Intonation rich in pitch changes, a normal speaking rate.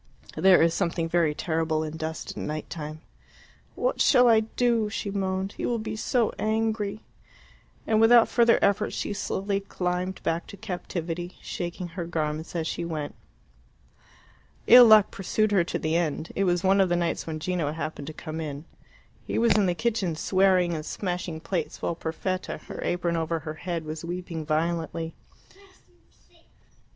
No: average, 3.8 semitones; average, 165 wpm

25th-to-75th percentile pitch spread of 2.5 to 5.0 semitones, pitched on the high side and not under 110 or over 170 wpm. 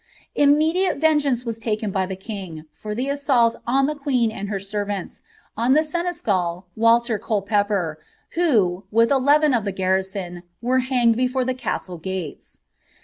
No: wide, 5.5 semitones; high, 230 Hz; average, 150 wpm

